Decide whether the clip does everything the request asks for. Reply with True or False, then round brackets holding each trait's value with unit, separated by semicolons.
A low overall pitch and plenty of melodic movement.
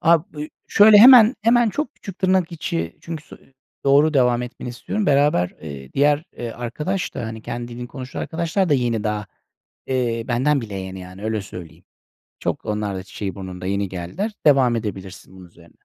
True (120 Hz; 8.1 semitones)